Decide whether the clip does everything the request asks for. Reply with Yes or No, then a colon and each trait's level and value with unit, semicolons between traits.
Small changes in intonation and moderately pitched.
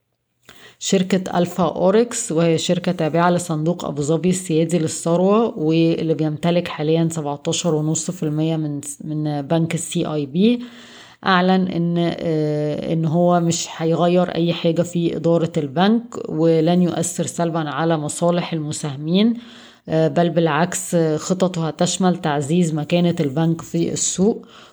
Yes: narrow, 1.8 semitones; medium, 170 Hz